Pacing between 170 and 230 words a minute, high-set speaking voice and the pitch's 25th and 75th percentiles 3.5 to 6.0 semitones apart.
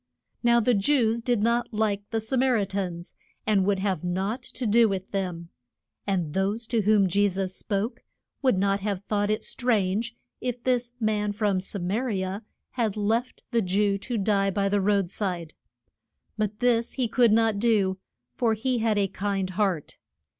No: average, 180 wpm; high, 205 Hz; average, 3.0 semitones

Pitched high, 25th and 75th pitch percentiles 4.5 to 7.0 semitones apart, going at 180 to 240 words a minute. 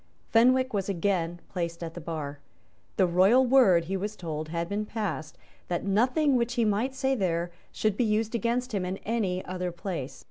Yes: high, 195 Hz; average, 5.2 semitones; average, 185 wpm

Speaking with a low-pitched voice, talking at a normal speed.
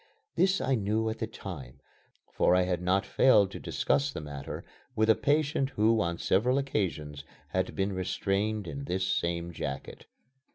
Yes: low, 100 Hz; average, 165 wpm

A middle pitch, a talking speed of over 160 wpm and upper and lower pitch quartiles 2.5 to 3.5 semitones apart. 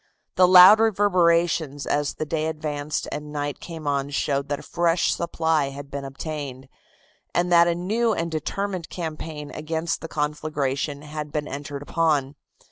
No: medium, 155 Hz; average, 155 wpm; average, 2.8 semitones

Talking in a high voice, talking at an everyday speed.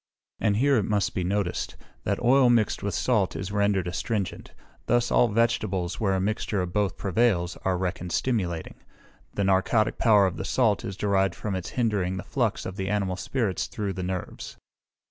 No: low, 100 Hz; average, 185 wpm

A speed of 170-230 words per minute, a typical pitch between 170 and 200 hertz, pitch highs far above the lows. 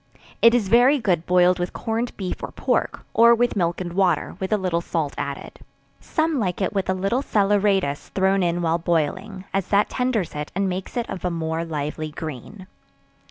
No: average, 195 wpm; medium, 185 Hz; average, 3.8 semitones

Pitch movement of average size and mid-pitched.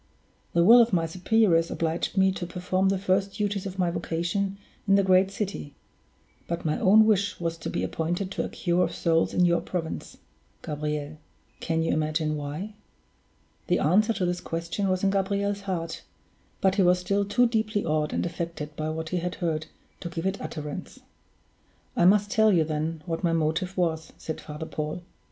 Yes: average, 3.3 semitones; medium, 175 Hz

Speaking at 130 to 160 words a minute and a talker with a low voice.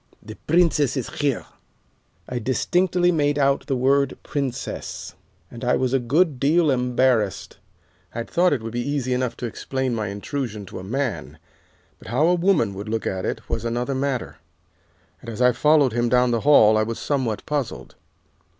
No: average, 180 wpm; low, 130 Hz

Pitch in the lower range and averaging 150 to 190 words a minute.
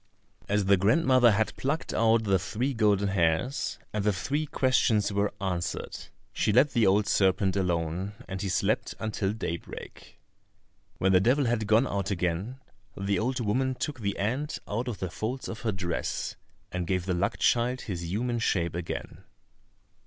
Yes: low, 105 Hz; average, 165 wpm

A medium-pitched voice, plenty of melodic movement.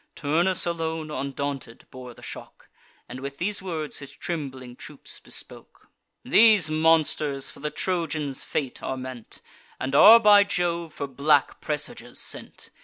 No: medium, 150 Hz; average, 3.7 semitones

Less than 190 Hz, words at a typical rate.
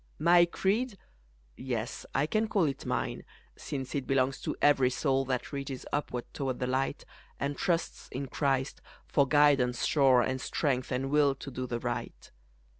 Yes: low, 135 Hz; average, 165 wpm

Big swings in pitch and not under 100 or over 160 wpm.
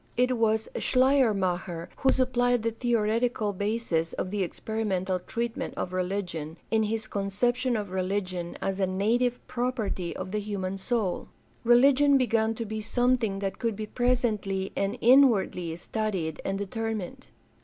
No: average, 4.0 semitones; average, 145 wpm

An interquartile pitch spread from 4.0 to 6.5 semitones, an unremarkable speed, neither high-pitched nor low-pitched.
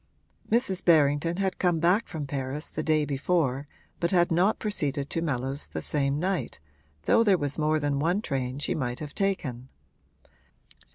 Yes: average, 4.3 semitones; average, 165 wpm; medium, 155 Hz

